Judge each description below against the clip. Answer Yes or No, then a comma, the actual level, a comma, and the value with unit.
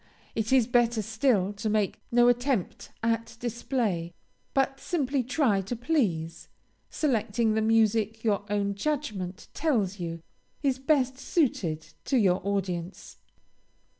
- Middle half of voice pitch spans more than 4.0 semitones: Yes, average, 4.6 semitones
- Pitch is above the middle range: Yes, high, 225 Hz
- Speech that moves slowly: Yes, slow, 125 wpm